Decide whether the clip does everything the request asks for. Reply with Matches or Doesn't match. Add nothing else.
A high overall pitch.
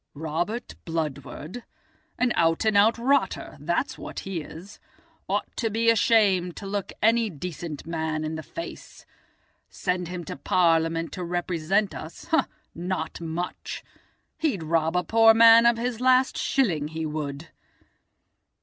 Doesn't match